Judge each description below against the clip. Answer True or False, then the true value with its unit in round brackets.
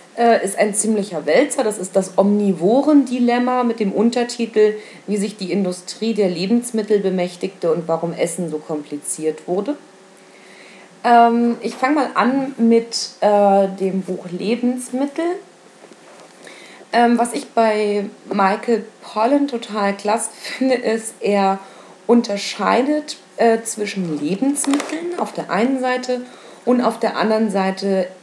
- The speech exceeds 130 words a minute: False (125 wpm)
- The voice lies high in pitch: True (220 Hz)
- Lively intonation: False (3.9 semitones)